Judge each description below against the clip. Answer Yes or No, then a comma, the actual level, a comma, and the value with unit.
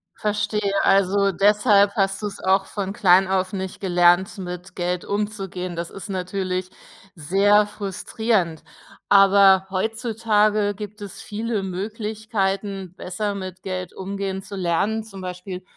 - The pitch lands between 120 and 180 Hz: No, high, 195 Hz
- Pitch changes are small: Yes, narrow, 2.0 semitones